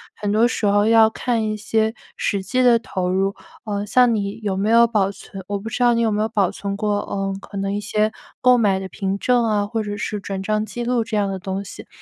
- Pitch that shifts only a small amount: Yes, narrow, 2.2 semitones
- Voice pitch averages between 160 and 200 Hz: No, high, 210 Hz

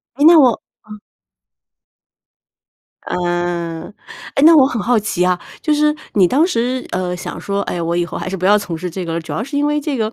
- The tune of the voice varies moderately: No, wide, 7.7 semitones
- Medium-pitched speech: No, high, 205 Hz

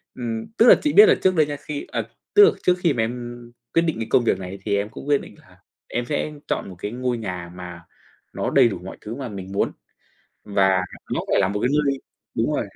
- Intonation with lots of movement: Yes, wide, 6.7 semitones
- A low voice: Yes, low, 120 Hz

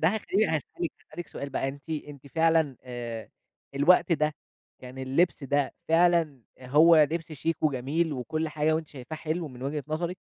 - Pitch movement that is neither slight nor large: Yes, average, 3.3 semitones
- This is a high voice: No, medium, 155 Hz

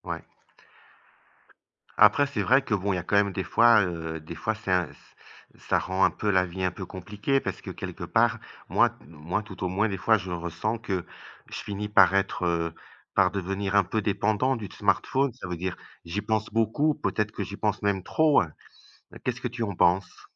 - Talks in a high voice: No, low, 100 Hz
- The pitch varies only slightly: No, average, 3.1 semitones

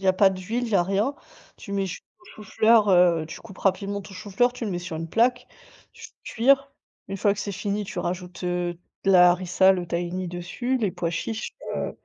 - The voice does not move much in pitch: No, average, 3.1 semitones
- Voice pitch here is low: No, high, 195 Hz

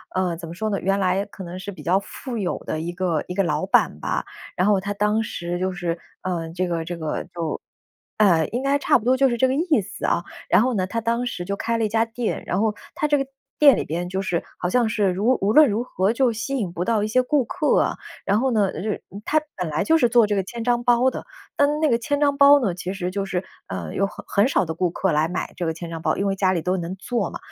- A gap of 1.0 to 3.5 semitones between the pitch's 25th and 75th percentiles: No, average, 5.0 semitones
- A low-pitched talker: No, high, 200 Hz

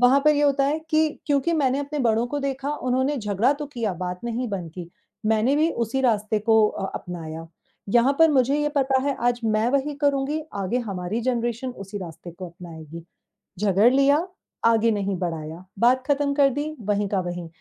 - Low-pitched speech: No, high, 240 Hz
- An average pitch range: No, wide, 6.1 semitones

